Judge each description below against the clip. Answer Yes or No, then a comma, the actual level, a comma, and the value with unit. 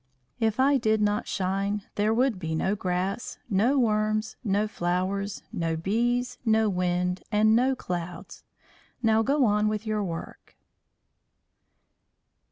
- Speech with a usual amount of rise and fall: Yes, average, 3.1 semitones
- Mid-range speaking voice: No, high, 210 Hz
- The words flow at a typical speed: No, slow, 130 wpm